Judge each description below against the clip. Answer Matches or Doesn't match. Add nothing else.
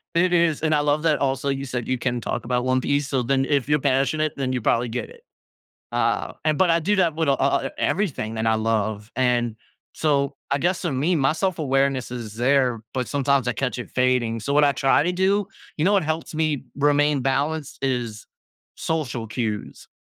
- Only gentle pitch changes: Doesn't match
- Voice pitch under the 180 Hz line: Matches